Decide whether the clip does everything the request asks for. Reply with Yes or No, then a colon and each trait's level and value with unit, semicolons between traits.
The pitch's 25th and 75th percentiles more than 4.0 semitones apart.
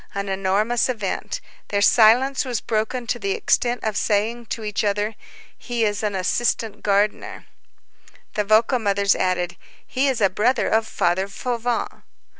No: average, 3.1 semitones